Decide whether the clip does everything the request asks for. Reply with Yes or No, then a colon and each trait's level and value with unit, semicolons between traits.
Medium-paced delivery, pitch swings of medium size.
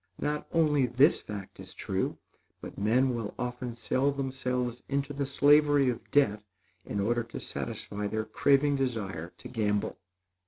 Yes: average, 150 wpm; average, 4.2 semitones